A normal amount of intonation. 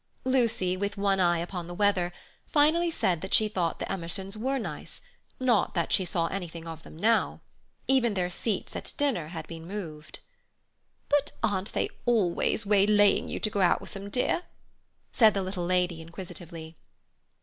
Yes: average, 3.8 semitones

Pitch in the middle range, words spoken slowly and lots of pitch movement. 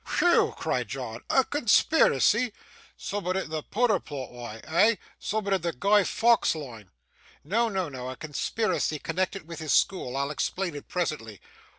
No: medium, 180 Hz; average, 160 wpm; wide, 6.7 semitones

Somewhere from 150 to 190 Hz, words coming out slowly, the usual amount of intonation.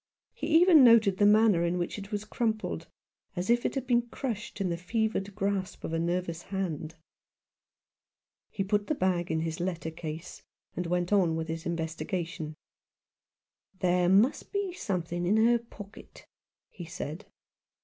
No: medium, 185 Hz; average, 160 wpm; average, 4.2 semitones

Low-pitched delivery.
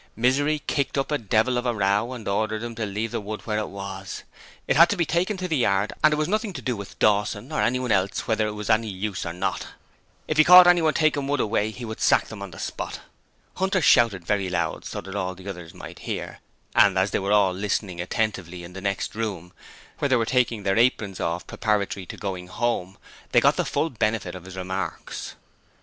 Yes: low, 105 Hz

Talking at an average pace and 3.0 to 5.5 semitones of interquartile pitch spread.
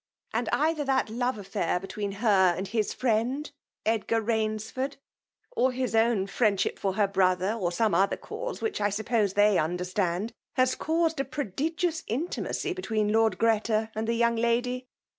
Yes: average, 170 wpm; average, 4.0 semitones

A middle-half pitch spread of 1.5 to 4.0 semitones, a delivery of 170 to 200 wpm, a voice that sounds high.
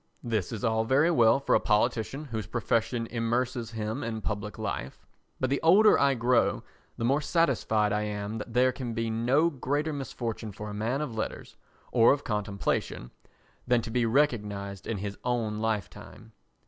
No: average, 3.2 semitones; average, 175 wpm; low, 115 Hz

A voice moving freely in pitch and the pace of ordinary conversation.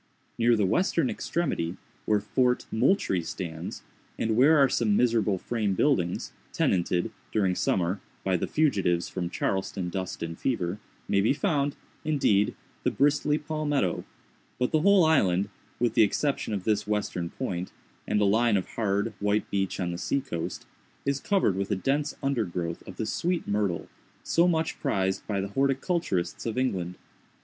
Yes: wide, 6.8 semitones; average, 155 wpm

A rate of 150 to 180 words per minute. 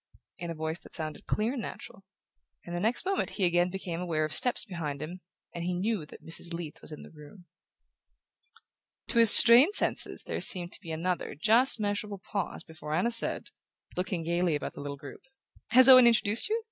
No: average, 195 wpm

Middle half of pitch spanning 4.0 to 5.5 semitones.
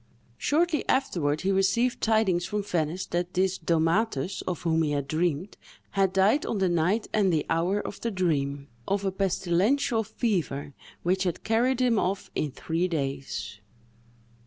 Yes: average, 4.4 semitones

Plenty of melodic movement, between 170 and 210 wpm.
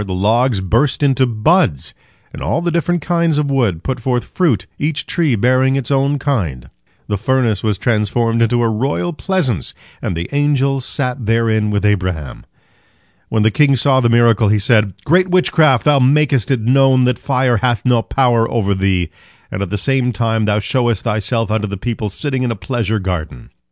No: average, 4.5 semitones; average, 185 wpm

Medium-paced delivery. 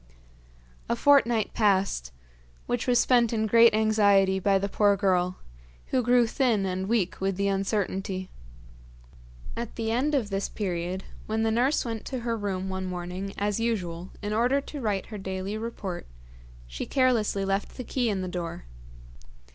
Yes: average, 165 wpm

